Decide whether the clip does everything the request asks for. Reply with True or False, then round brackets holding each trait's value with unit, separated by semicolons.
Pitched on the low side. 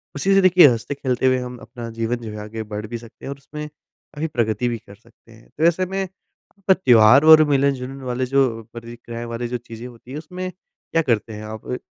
True (125 Hz)